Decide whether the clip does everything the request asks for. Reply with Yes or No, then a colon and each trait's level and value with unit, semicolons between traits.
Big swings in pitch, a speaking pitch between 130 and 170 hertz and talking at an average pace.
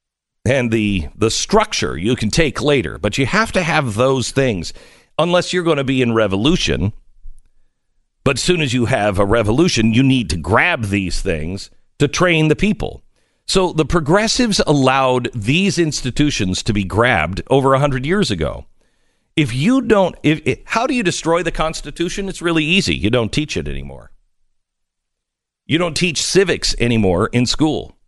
Yes: wide, 7.4 semitones; low, 135 Hz; average, 170 wpm